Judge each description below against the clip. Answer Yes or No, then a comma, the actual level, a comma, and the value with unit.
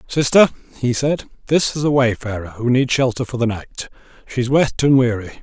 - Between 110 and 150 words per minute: No, average, 200 wpm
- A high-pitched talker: No, low, 125 Hz